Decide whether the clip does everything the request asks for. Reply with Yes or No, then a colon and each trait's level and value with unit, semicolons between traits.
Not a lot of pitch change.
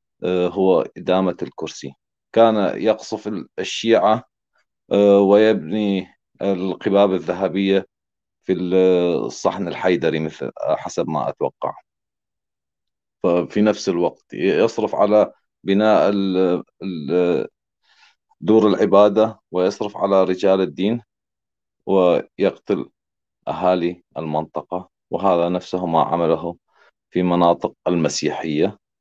Yes: narrow, 2.0 semitones